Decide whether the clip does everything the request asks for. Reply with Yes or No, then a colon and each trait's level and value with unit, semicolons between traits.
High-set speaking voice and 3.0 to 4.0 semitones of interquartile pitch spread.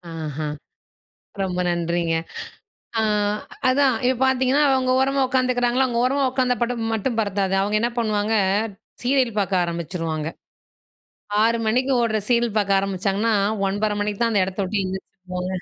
No: high, 215 Hz; average, 4.8 semitones